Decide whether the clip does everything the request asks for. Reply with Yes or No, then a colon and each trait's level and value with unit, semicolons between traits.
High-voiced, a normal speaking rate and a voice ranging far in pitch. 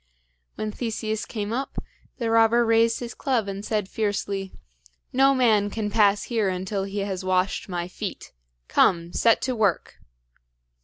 No: high, 210 Hz; average, 150 wpm; average, 2.7 semitones